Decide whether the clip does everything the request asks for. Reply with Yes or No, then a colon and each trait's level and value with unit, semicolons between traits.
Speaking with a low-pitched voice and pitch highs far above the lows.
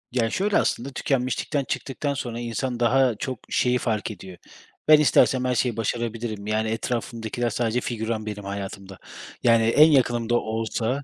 No: low, 120 Hz; narrow, 2.5 semitones